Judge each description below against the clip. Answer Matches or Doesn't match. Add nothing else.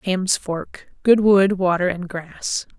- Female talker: Matches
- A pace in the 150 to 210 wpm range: Doesn't match